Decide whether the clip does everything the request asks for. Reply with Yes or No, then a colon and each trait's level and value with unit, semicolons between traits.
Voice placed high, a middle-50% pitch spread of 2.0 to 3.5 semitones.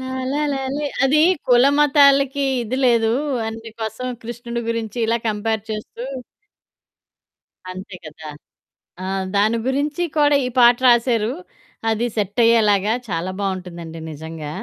No: high, 230 Hz; average, 4.3 semitones